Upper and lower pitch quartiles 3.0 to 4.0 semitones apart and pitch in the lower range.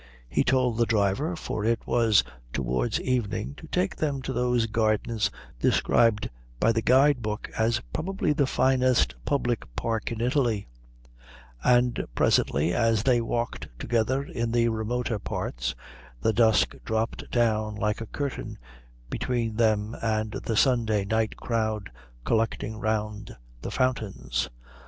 No: narrow, 2.5 semitones; low, 115 Hz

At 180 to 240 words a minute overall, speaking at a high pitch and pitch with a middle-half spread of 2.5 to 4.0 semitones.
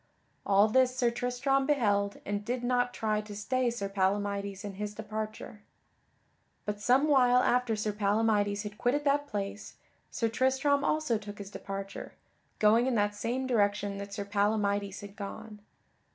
No: average, 155 wpm; high, 215 Hz; average, 3.4 semitones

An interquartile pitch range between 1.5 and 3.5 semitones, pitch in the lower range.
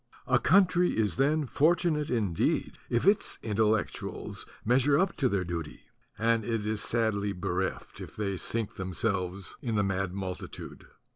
No: average, 5.3 semitones; low, 110 Hz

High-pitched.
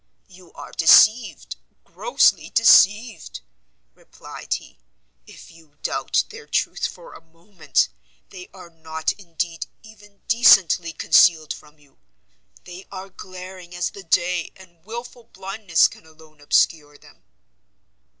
No: medium, 180 Hz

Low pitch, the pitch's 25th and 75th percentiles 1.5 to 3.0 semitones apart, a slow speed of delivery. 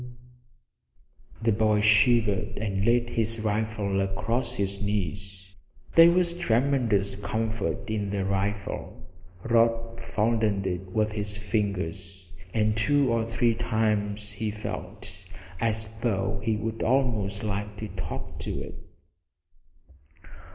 Yes: low, 105 Hz; narrow, 2.4 semitones; slow, 115 wpm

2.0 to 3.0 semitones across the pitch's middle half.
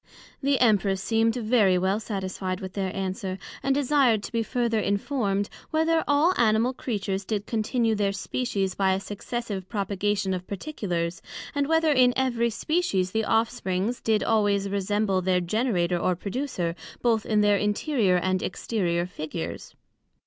No: average, 4.0 semitones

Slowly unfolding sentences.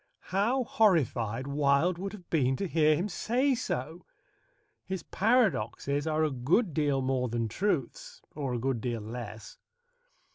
No: average, 145 wpm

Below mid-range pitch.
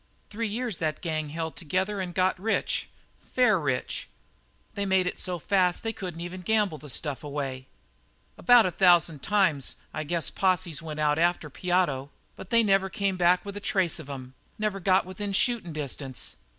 No: medium, 180 Hz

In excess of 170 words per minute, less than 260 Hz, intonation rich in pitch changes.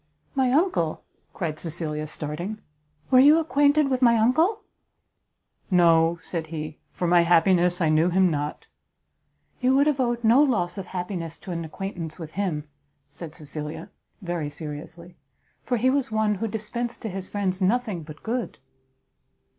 No: average, 155 wpm; medium, 185 Hz; wide, 6.6 semitones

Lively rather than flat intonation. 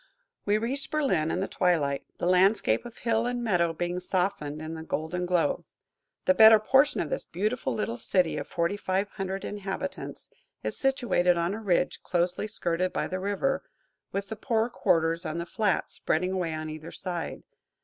No: average, 4.4 semitones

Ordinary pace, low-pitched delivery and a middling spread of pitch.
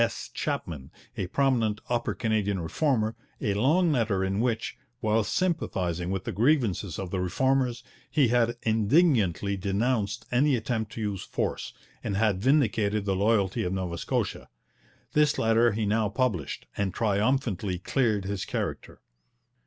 Yes: average, 145 wpm; low, 110 Hz; average, 4.0 semitones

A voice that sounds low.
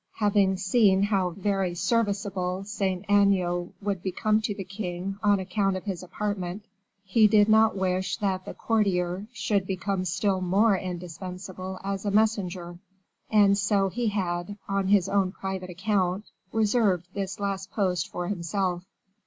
No: high, 195 Hz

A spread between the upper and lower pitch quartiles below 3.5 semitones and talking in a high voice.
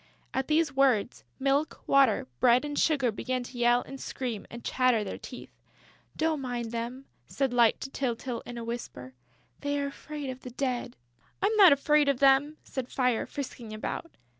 Yes: average, 2.7 semitones; very high, 260 Hz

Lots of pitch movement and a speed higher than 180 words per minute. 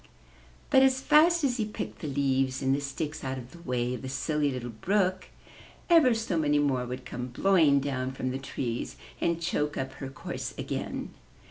Yes: wide, 5.9 semitones; average, 195 wpm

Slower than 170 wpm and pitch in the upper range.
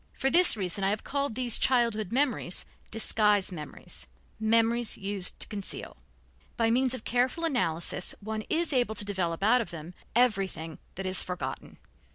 Yes: average, 160 wpm; high, 215 Hz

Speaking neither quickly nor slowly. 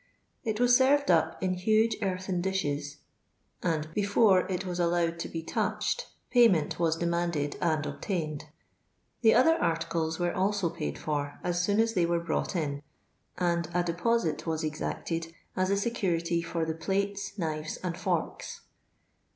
Yes: average, 155 wpm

